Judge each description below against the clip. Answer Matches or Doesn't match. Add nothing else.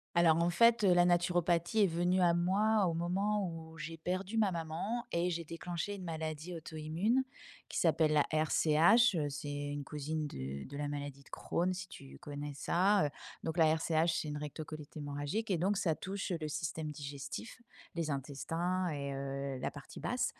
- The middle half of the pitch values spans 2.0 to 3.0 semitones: Doesn't match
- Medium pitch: Matches